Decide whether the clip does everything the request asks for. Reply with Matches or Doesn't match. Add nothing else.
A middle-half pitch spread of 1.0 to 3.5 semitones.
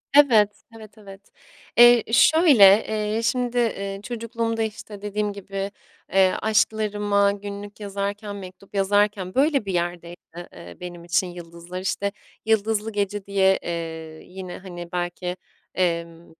Matches